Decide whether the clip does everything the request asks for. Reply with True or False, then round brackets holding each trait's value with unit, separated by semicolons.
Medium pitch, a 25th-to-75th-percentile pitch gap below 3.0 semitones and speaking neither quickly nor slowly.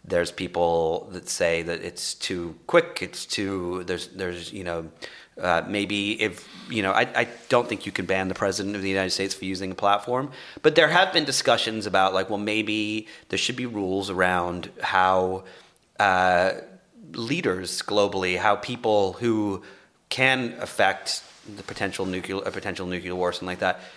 False (95 Hz; 2.5 semitones; 175 wpm)